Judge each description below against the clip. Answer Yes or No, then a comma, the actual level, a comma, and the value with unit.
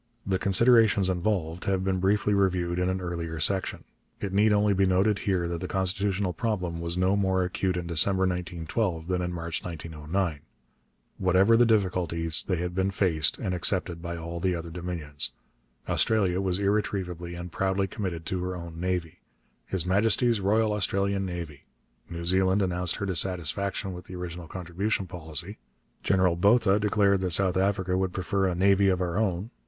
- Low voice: Yes, very low, 95 Hz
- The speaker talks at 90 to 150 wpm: No, average, 170 wpm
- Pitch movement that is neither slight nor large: No, narrow, 2.2 semitones